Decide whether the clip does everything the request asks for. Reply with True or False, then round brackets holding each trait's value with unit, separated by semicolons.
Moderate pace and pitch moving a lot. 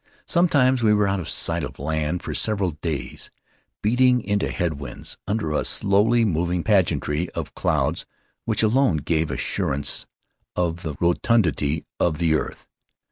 True (145 wpm; 5.7 semitones)